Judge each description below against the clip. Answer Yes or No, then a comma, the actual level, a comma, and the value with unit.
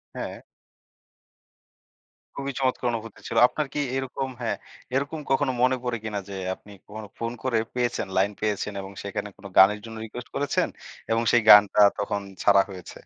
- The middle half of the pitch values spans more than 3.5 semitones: Yes, average, 3.9 semitones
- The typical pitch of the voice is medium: No, low, 115 Hz